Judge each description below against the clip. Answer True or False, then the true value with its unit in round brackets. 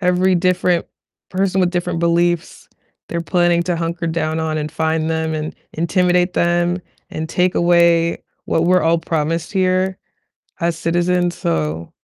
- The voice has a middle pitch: True (170 Hz)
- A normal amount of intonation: False (1.7 semitones)